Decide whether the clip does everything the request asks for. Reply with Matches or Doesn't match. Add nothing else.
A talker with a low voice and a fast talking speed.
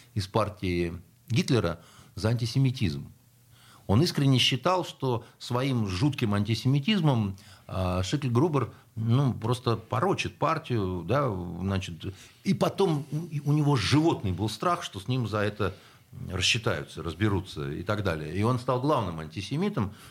Doesn't match